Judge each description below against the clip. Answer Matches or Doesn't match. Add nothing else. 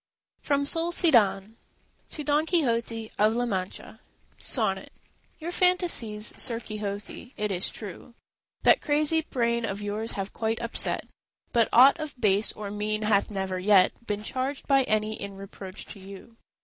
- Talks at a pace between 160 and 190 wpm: Doesn't match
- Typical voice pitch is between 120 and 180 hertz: Doesn't match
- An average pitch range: Matches